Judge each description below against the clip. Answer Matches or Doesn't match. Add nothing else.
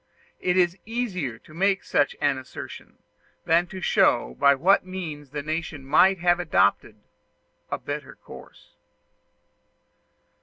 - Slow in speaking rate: Matches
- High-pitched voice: Doesn't match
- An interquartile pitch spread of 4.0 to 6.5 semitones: Matches